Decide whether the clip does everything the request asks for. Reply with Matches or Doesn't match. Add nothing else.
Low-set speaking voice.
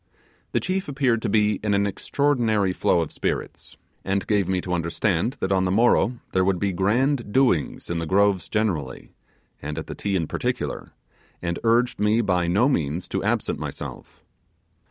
Matches